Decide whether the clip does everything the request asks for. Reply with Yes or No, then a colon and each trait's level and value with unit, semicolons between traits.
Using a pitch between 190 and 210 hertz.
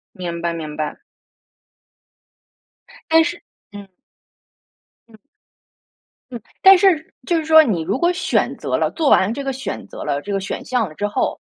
No: high, 230 Hz